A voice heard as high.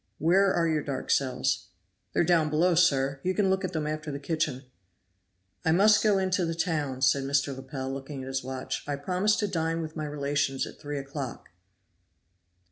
No: medium, 150 Hz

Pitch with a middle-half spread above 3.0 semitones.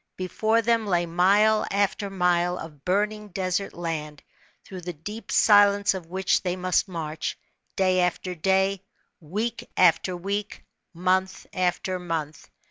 No: narrow, 2.4 semitones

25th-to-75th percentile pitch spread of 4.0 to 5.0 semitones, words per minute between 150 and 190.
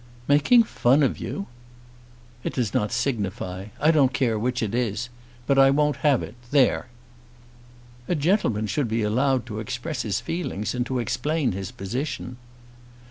Yes: average, 4.7 semitones; average, 155 wpm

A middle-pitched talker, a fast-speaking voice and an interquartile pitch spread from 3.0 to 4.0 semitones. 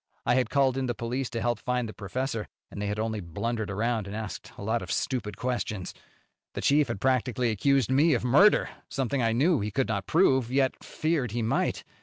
No: low, 120 Hz; fast, 215 wpm; average, 3.4 semitones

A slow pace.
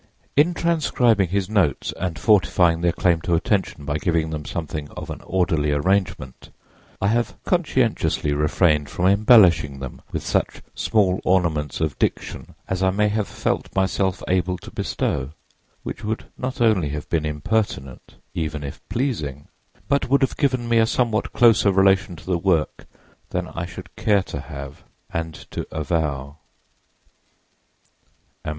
No: average, 150 wpm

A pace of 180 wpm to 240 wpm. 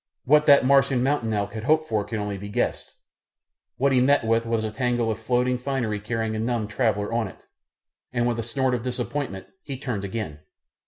Yes: fast, 205 wpm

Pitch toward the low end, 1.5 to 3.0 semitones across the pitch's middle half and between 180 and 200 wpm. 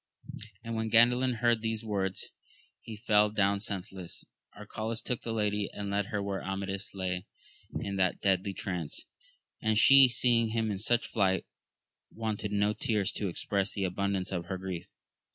No: low, 105 Hz; narrow, 2.5 semitones; average, 160 wpm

